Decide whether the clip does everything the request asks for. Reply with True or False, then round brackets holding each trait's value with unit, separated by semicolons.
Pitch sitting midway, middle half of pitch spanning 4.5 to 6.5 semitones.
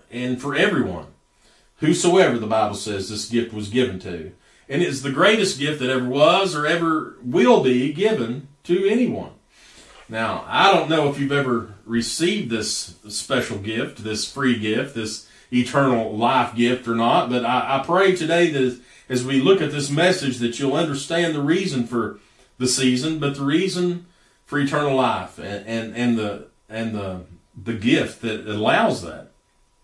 False (125 Hz; 5.2 semitones)